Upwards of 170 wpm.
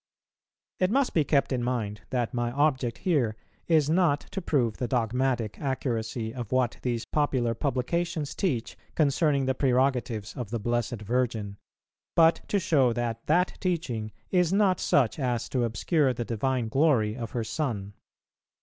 No: average, 160 wpm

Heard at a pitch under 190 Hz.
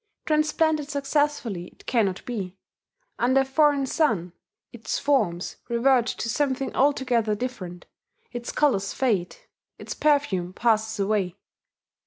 No: high, 240 Hz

